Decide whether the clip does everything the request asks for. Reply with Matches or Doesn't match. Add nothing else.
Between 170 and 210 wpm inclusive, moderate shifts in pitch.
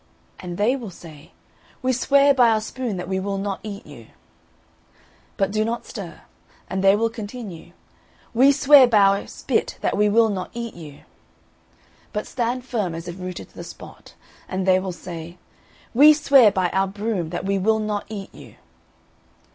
Matches